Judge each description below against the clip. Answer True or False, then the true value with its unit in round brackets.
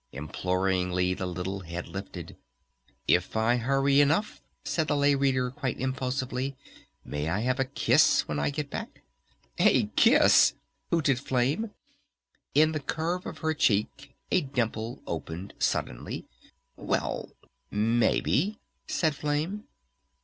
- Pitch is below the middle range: True (130 Hz)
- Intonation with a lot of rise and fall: True (6.9 semitones)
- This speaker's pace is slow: True (125 wpm)